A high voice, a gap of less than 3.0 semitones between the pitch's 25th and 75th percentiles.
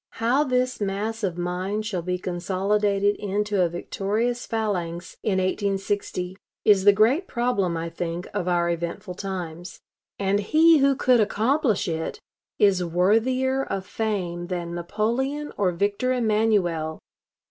No: high, 200 Hz; average, 3.9 semitones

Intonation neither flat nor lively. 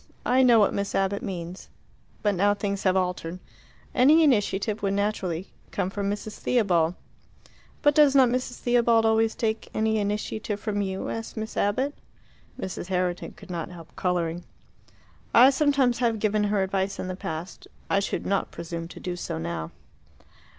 Yes: average, 3.6 semitones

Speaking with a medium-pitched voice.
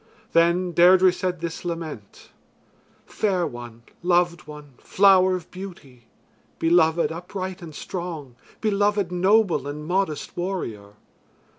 Yes: medium, 175 Hz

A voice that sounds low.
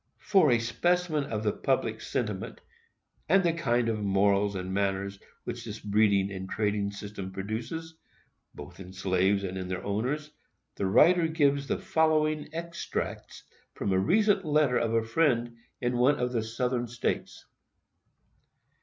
Yes: low, 115 Hz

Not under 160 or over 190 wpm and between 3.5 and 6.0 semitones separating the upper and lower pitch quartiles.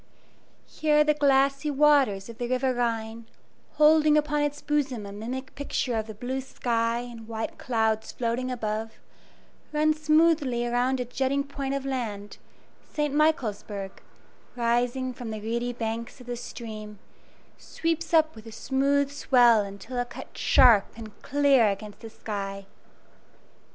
No: average, 145 wpm; average, 4.0 semitones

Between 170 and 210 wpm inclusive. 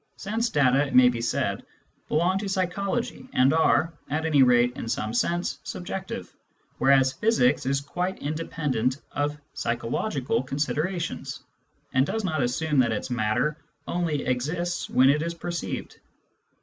No: average, 140 wpm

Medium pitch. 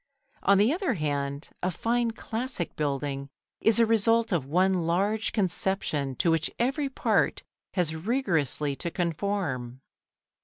Yes: medium, 180 Hz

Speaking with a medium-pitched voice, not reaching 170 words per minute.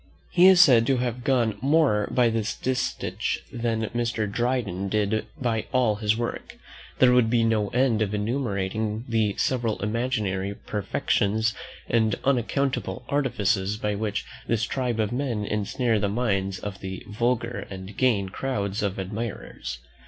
No: low, 110 Hz; average, 145 wpm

